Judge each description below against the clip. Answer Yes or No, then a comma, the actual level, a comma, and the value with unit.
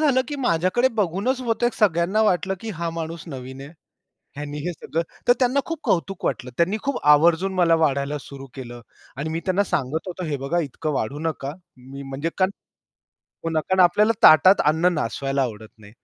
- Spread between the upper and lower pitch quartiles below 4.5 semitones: No, wide, 5.5 semitones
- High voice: No, medium, 165 Hz